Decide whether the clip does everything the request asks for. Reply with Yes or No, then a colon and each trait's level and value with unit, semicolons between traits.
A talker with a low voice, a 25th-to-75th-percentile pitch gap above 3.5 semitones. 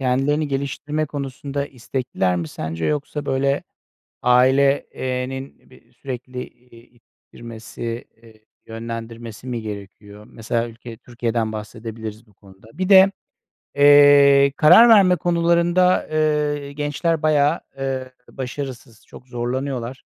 Yes: low, 130 Hz; average, 3.9 semitones